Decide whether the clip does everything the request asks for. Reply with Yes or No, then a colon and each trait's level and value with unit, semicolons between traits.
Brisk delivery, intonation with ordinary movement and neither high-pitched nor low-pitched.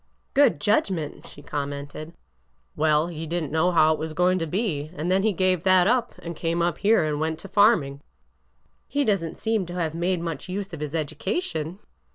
Yes: fast, 220 wpm; average, 3.4 semitones; medium, 170 Hz